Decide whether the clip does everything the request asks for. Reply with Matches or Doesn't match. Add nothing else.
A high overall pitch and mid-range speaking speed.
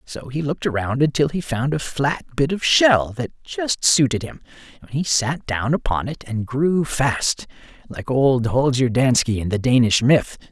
Doesn't match